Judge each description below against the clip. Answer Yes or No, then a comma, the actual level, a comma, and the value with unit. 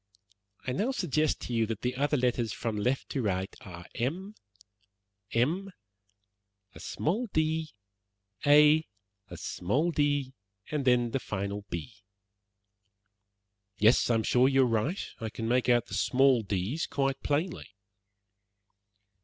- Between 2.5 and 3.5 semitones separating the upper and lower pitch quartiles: No, average, 4.9 semitones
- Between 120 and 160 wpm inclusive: Yes, average, 145 wpm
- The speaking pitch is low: Yes, low, 130 Hz